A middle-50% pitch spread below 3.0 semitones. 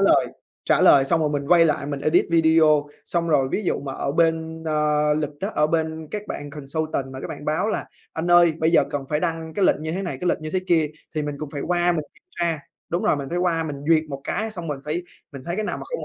Yes: narrow, 2.4 semitones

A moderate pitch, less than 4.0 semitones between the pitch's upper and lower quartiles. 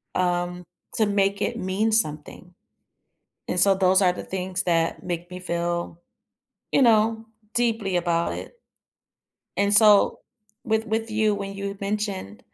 No: high, 195 Hz; average, 3.3 semitones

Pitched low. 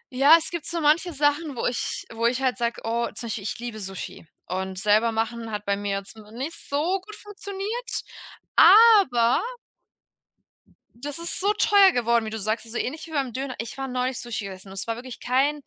No: high, 245 Hz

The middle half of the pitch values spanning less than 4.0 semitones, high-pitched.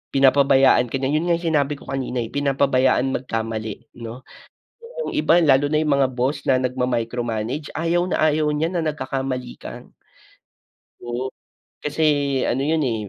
No: average, 3.2 semitones; low, 135 Hz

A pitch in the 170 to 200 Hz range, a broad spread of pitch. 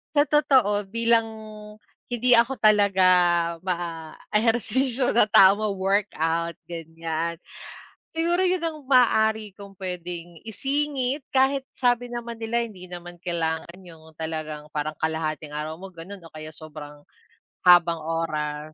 Yes: high, 190 Hz; wide, 6.3 semitones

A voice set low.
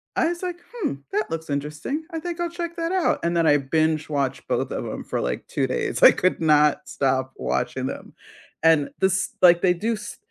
No: medium, 170 Hz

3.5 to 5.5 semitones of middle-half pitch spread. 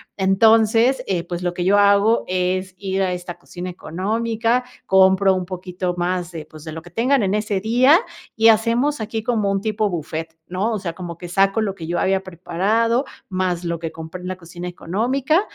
Yes: average, 3.9 semitones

